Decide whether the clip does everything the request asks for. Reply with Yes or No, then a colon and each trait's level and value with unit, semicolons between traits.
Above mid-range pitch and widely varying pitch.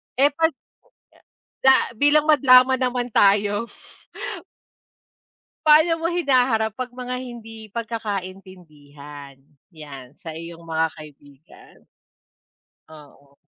Yes: high, 220 Hz; wide, 8.2 semitones